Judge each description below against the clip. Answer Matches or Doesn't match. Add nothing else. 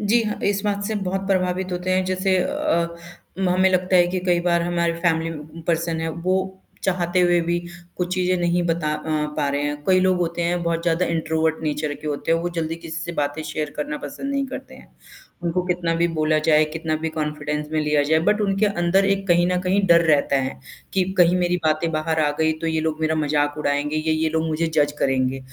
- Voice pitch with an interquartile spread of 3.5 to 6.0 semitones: Doesn't match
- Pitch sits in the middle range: Matches